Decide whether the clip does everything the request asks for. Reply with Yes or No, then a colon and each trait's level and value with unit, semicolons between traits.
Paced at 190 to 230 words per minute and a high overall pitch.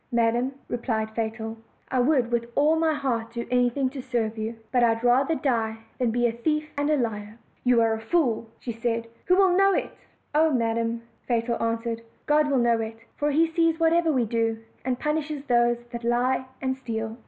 Yes: average, 200 wpm; high, 240 Hz